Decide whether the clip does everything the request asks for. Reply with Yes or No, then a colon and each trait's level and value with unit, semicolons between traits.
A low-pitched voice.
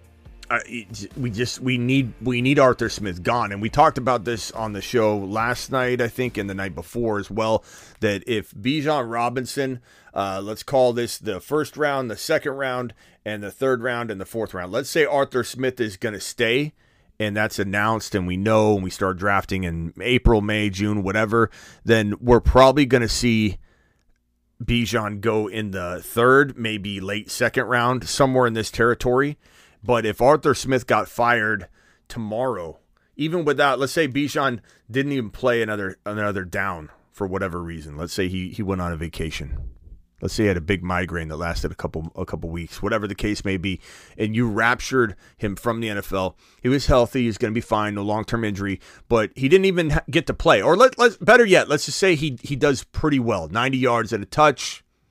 Yes: low, 110 Hz